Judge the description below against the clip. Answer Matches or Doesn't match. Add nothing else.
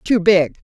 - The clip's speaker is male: Doesn't match